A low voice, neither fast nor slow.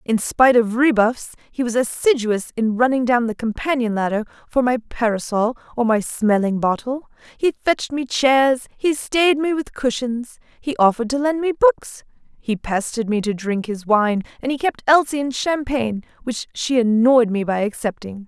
No: high, 245 Hz; average, 175 wpm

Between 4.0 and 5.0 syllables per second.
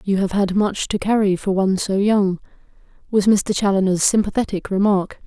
No: 5.2 syllables/s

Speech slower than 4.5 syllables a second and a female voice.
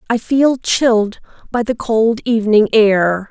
Yes: 4.0 syllables/s; female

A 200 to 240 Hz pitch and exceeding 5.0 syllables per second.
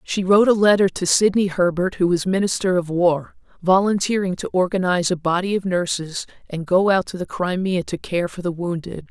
No: medium, 185 Hz; 5.4 syllables/s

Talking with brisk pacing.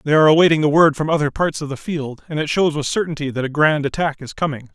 Yes: fast, 280 wpm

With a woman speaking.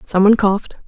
Yes: female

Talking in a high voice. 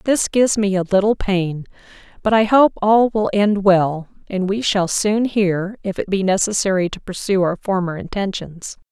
Yes: high, 195 Hz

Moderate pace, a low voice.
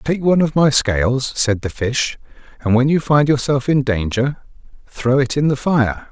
Yes: average, 195 wpm; low, 130 Hz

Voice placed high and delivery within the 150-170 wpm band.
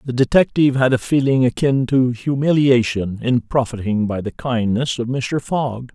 No: low, 125 Hz; average, 160 wpm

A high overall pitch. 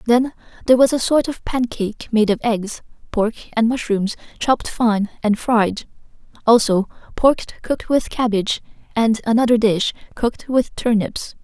Yes: high, 230 Hz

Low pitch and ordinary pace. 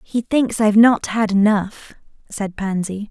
No: high, 210 Hz; average, 155 wpm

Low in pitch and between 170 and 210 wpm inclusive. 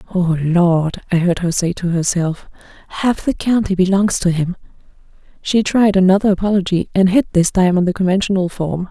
No: medium, 185 Hz; average, 175 wpm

